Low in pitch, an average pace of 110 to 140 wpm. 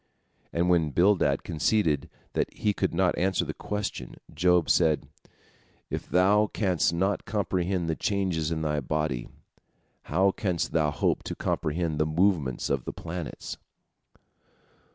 Yes: very low, 85 Hz; slow, 135 wpm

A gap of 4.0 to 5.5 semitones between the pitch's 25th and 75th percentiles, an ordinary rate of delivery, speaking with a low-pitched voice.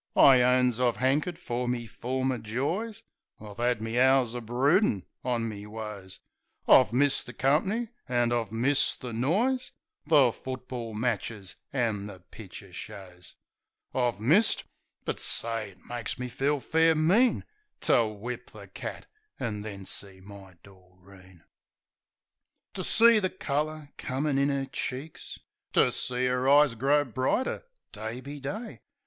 Yes: average, 4.6 semitones; average, 145 wpm; low, 125 Hz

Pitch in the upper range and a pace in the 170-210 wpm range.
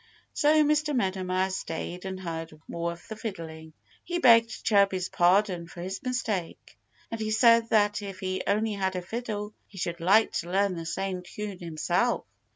Yes: high, 195 Hz; average, 175 wpm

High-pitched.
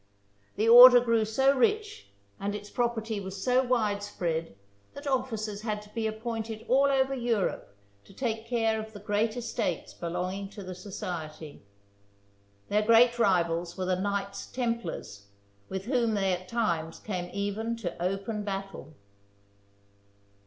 Yes: high, 210 Hz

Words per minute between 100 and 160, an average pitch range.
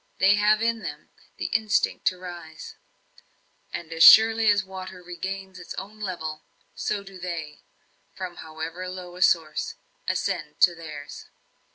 Yes: average, 145 wpm; average, 3.1 semitones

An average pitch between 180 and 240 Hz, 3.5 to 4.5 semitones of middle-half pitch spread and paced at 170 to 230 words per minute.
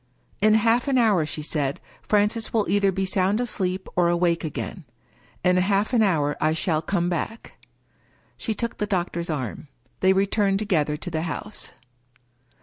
Yes: high, 190 Hz; average, 3.9 semitones; average, 175 wpm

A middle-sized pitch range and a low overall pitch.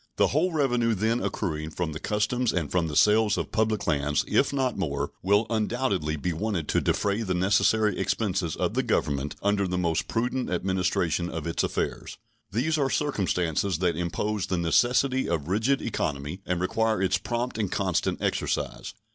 Yes: average, 4.8 semitones; low, 100 Hz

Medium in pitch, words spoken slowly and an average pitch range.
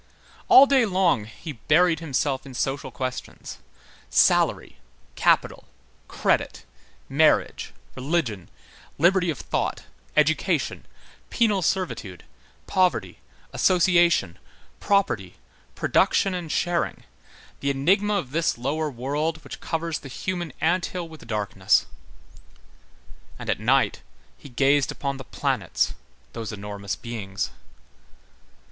No: medium, 150 Hz; slow, 105 wpm; wide, 5.8 semitones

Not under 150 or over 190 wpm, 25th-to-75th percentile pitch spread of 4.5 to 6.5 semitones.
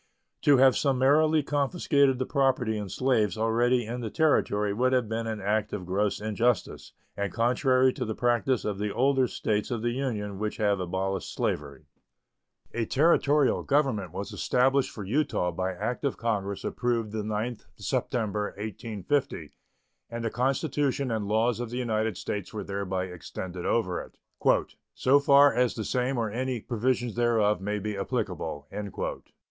No: average, 160 wpm; average, 3.8 semitones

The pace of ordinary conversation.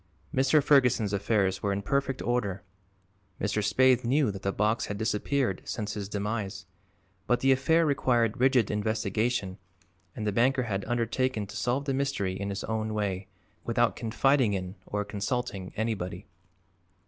Yes: average, 150 wpm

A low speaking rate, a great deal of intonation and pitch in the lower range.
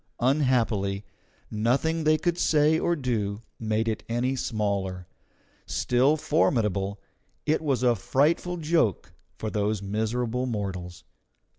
Yes: slow, 115 wpm; wide, 6.0 semitones; low, 120 Hz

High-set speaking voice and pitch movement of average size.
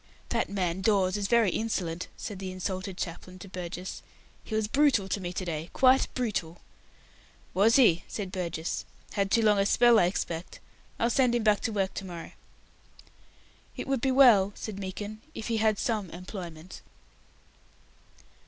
Yes: high, 195 Hz; average, 3.5 semitones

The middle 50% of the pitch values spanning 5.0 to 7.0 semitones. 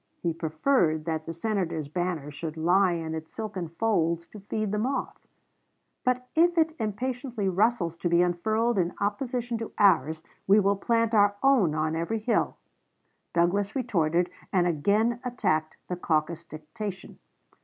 Yes: average, 5.3 semitones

